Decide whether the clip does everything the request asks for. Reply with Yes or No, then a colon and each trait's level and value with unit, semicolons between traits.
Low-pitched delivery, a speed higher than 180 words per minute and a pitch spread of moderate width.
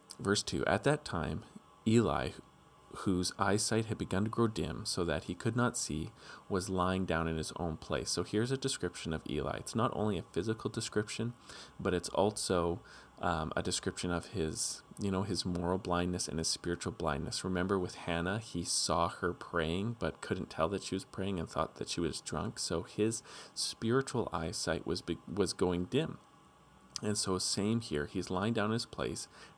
Yes: very low, 95 Hz; average, 190 wpm; average, 4.0 semitones